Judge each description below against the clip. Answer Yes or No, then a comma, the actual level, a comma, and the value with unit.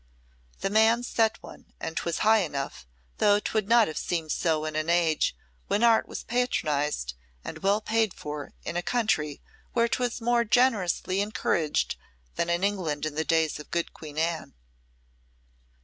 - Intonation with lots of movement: Yes, wide, 6.0 semitones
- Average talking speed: Yes, average, 160 wpm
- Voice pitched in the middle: Yes, medium, 175 Hz